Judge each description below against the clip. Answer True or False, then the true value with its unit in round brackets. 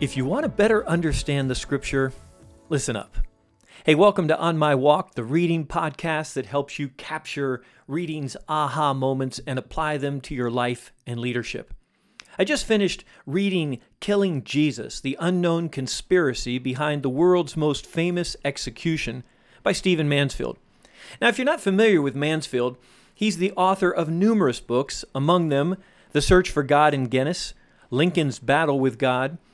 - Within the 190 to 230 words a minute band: False (155 wpm)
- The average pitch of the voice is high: False (150 Hz)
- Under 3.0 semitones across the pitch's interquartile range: False (4.8 semitones)